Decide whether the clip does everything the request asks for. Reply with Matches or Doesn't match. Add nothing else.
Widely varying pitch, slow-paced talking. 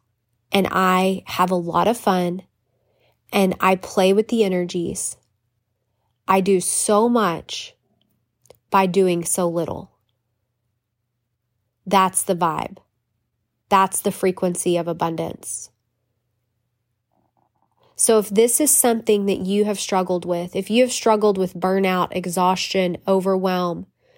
Matches